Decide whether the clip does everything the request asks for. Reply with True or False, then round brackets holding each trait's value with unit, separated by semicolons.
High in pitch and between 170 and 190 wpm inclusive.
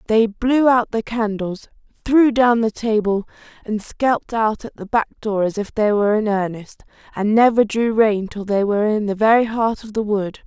False (215 Hz; 205 wpm)